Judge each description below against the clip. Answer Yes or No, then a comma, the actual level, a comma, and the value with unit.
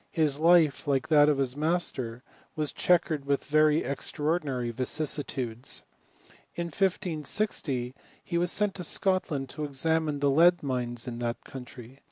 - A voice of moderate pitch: Yes, medium, 145 Hz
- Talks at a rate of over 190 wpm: No, average, 150 wpm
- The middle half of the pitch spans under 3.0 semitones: No, average, 4.0 semitones